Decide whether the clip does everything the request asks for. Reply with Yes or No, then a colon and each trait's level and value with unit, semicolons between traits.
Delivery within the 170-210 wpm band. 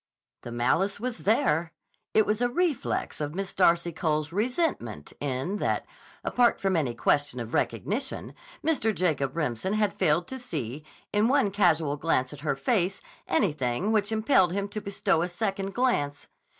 No: average, 160 wpm